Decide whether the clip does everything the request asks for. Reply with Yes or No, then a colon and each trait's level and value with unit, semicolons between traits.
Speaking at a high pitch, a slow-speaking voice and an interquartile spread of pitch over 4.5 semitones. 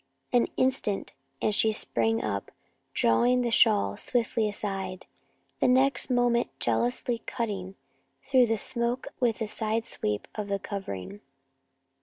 No: high, 225 Hz; slow, 130 wpm; average, 3.5 semitones